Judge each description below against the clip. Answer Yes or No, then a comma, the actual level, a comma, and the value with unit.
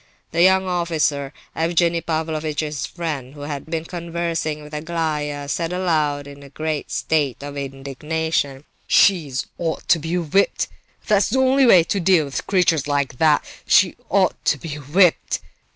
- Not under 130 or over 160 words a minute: Yes, average, 145 wpm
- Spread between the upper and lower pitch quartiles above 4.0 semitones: No, average, 2.9 semitones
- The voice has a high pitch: No, medium, 160 Hz